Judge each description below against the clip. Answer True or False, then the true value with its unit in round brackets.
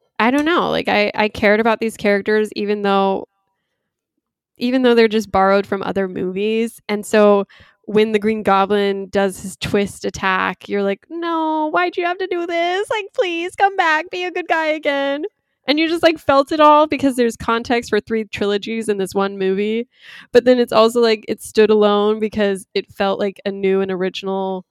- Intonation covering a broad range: True (6.3 semitones)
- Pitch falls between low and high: False (215 Hz)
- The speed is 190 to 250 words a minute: True (195 wpm)